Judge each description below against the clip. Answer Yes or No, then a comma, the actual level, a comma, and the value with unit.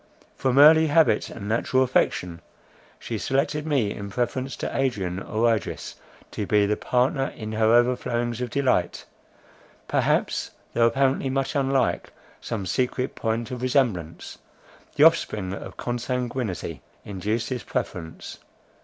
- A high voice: No, low, 120 Hz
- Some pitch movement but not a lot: Yes, average, 4.0 semitones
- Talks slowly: Yes, slow, 130 wpm